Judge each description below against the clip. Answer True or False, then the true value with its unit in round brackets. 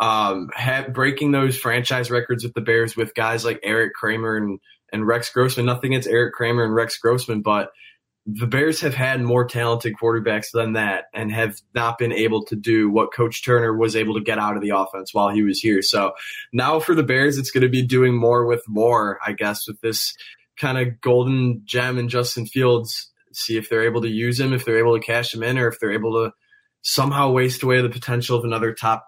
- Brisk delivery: True (225 wpm)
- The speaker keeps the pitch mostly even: True (2.0 semitones)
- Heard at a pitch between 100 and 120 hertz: True (115 Hz)